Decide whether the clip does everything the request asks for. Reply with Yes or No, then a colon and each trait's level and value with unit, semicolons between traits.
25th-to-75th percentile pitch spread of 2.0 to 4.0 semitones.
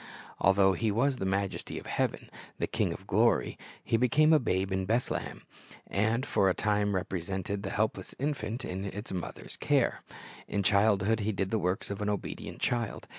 Yes: average, 2.7 semitones